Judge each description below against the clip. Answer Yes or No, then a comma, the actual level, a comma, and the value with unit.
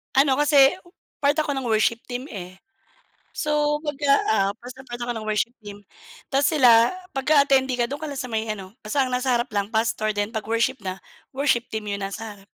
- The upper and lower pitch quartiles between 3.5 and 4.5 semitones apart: Yes, average, 4.1 semitones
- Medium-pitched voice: No, high, 240 Hz